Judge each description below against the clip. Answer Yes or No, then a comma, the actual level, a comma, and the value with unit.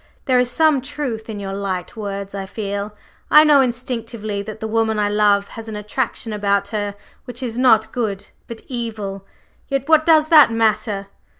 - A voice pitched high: Yes, high, 220 Hz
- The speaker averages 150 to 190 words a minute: Yes, average, 180 wpm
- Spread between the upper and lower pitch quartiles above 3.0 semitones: Yes, average, 3.5 semitones